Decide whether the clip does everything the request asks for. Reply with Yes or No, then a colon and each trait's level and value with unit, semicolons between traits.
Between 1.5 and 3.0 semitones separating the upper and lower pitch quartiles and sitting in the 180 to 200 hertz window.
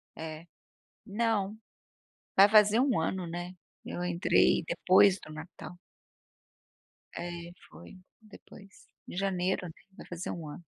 Yes: narrow, 2.6 semitones; medium, 185 Hz